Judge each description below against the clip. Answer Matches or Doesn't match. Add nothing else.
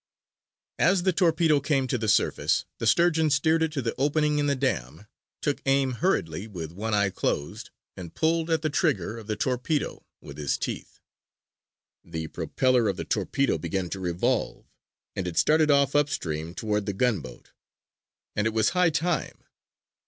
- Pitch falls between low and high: Doesn't match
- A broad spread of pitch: Matches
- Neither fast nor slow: Matches